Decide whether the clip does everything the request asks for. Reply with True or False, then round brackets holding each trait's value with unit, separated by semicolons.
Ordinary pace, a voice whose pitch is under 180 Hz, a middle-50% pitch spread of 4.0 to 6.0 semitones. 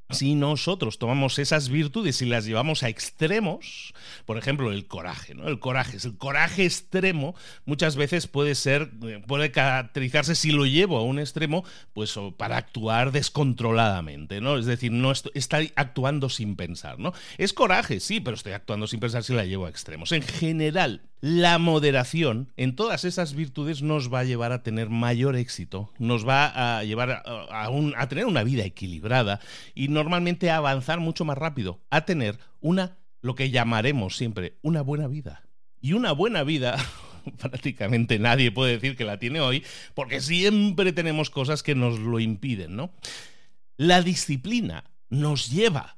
True (165 wpm; 135 Hz; 4.6 semitones)